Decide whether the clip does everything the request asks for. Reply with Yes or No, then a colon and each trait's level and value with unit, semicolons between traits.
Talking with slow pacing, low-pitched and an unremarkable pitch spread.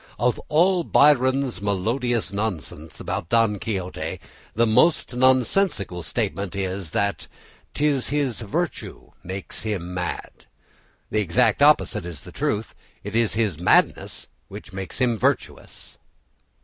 Yes: slow, 125 wpm; low, 110 Hz; average, 5.0 semitones